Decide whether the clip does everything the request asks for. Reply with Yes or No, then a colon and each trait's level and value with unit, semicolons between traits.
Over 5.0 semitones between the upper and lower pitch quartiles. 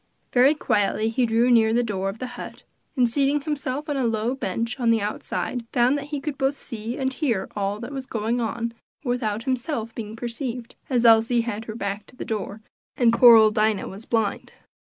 No: average, 2.8 semitones